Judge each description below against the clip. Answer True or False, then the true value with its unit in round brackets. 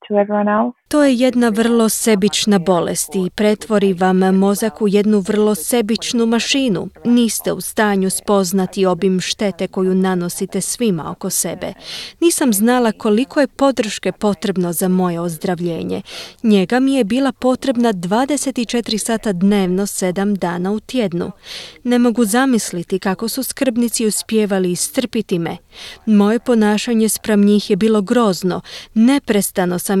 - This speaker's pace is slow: False (130 wpm)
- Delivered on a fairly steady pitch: False (3.9 semitones)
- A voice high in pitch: True (210 Hz)